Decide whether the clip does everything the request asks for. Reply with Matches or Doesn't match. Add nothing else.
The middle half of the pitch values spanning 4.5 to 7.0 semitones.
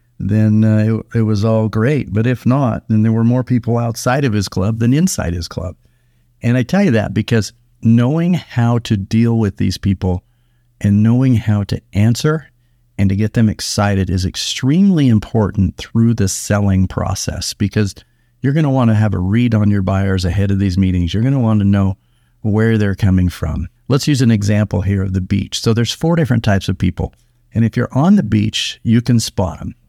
Doesn't match